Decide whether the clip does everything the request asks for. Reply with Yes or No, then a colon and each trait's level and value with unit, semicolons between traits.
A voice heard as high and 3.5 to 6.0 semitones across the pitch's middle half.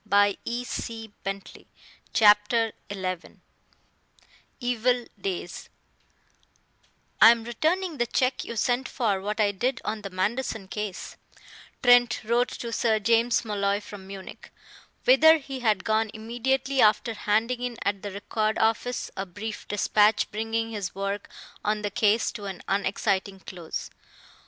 No: high, 220 Hz; average, 2.9 semitones